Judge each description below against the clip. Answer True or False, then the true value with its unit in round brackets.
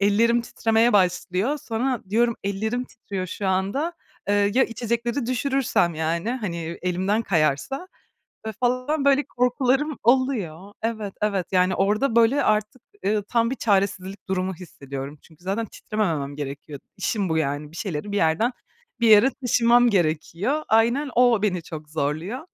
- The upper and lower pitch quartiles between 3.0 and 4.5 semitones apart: False (5.0 semitones)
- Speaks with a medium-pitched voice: False (210 Hz)